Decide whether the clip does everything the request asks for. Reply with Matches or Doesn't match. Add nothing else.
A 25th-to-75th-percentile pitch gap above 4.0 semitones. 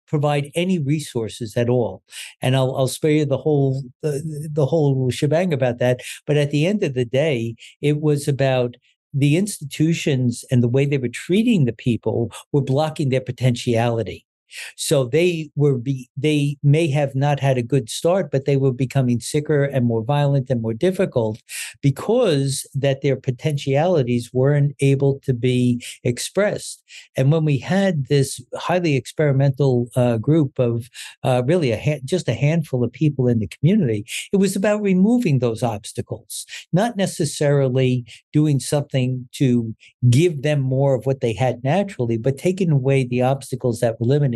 Doesn't match